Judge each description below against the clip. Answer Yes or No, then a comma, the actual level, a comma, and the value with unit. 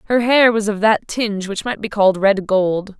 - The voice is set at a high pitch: Yes, high, 210 Hz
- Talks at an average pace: No, fast, 240 wpm